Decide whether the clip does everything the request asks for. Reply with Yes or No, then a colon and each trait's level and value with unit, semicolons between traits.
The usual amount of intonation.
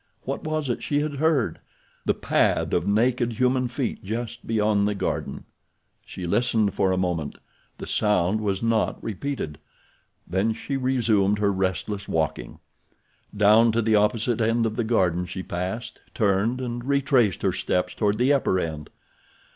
Yes: average, 4.0 semitones